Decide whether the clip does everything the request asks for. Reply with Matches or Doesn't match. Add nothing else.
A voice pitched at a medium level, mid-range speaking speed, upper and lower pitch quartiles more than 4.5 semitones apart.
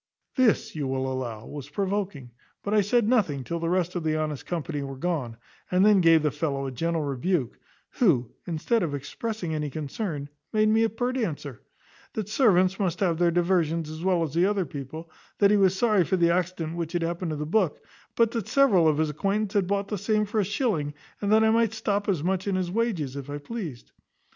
Doesn't match